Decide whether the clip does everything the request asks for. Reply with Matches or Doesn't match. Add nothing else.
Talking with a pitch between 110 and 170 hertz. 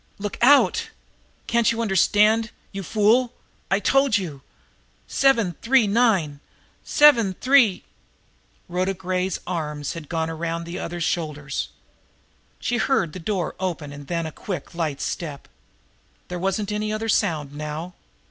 Doesn't match